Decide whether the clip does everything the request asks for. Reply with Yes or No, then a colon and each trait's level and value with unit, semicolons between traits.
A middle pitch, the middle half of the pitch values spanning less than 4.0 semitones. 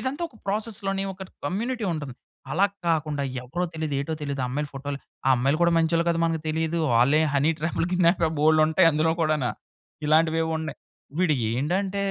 Yes: medium, 160 Hz; average, 3.2 semitones